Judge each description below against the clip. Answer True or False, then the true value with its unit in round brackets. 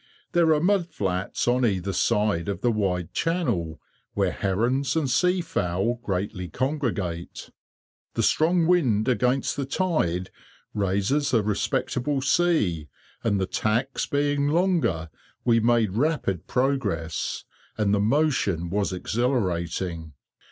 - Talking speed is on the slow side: True (125 wpm)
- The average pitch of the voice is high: False (115 Hz)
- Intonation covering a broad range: True (7.3 semitones)